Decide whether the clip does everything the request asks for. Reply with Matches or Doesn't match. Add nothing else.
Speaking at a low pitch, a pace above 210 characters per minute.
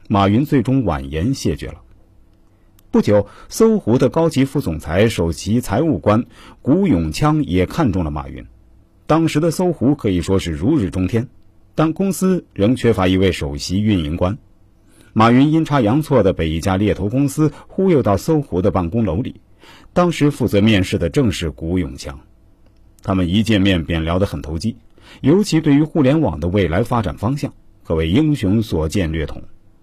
Matches